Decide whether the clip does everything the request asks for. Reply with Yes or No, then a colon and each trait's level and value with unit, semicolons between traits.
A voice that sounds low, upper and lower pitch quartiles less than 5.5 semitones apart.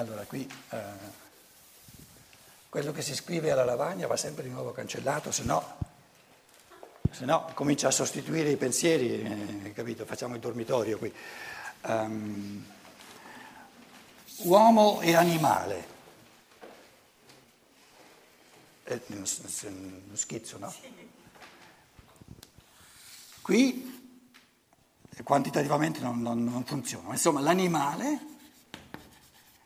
No: low, 125 Hz; wide, 7.7 semitones